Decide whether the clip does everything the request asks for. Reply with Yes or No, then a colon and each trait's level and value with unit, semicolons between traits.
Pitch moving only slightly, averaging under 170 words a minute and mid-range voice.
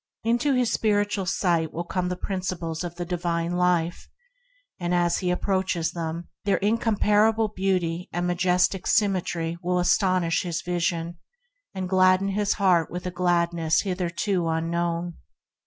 Yes: narrow, 2.1 semitones; average, 140 wpm; medium, 180 Hz